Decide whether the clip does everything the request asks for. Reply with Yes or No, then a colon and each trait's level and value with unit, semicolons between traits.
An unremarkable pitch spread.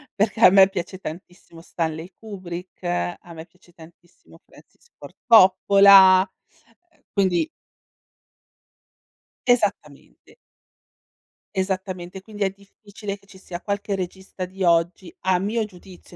No: narrow, 2.2 semitones